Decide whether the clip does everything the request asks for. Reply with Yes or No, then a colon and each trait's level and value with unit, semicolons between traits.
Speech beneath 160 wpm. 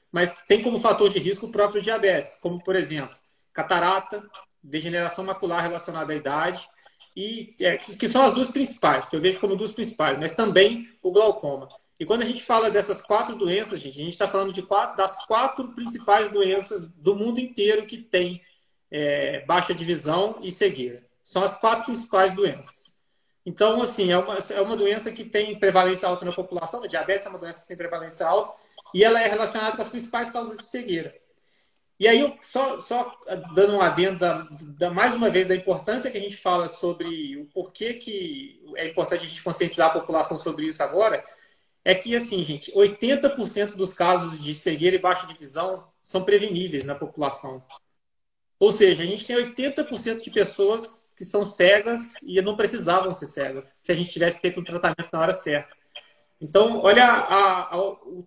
No: fast, 185 wpm